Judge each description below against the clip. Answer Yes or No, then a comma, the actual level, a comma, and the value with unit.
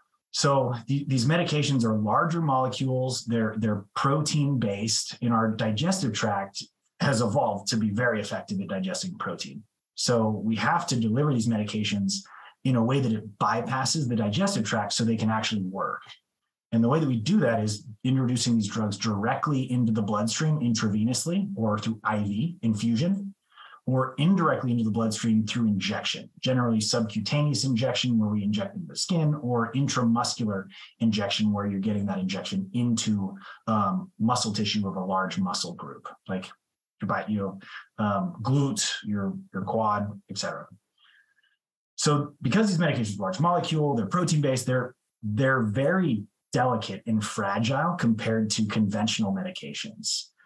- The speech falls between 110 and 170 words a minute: Yes, average, 150 wpm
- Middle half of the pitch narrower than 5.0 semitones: No, wide, 5.4 semitones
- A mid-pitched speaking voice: No, low, 120 Hz